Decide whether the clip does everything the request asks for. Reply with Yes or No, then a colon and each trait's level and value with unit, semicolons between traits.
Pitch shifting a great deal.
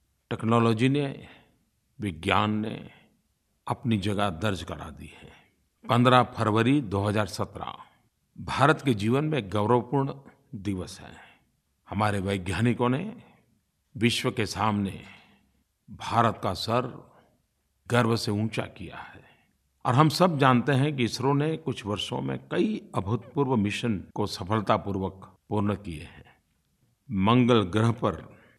No: average, 4.2 semitones